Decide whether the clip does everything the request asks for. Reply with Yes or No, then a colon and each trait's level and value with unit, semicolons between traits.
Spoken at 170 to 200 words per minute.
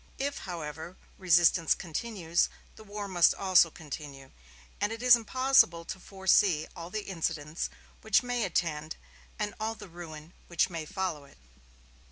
No: average, 145 wpm